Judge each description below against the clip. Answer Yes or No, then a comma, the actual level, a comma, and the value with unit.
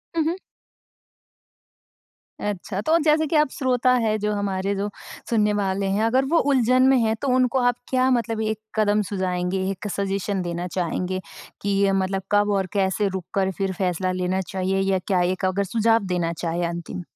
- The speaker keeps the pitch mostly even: No, average, 3.4 semitones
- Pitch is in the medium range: No, high, 200 Hz